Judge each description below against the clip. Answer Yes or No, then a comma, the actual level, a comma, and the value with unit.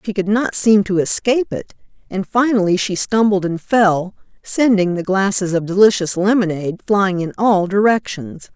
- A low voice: No, high, 200 Hz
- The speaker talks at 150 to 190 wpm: Yes, average, 160 wpm